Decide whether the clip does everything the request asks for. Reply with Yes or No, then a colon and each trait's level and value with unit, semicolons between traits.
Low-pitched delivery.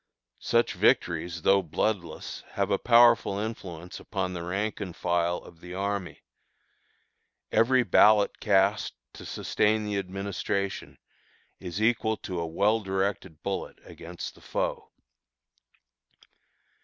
Yes: low, 100 Hz